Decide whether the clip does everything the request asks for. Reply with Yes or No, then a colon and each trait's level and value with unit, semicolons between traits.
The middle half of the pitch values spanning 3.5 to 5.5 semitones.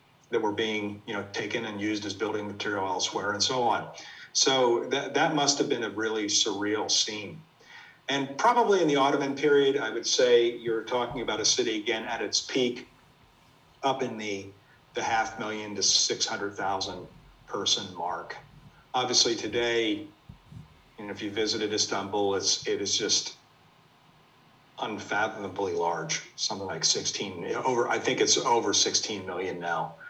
Yes: average, 4.6 semitones